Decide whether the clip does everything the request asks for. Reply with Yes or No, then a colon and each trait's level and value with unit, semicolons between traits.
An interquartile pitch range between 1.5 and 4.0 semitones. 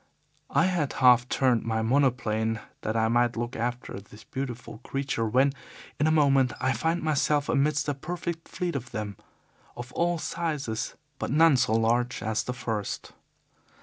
No: average, 4.4 semitones